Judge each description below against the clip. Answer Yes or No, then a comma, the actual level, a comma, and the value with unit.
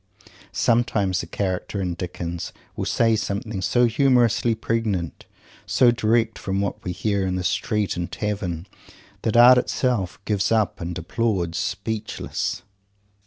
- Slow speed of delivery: Yes, slow, 130 wpm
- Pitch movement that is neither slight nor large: Yes, average, 4.0 semitones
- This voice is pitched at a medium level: No, low, 100 Hz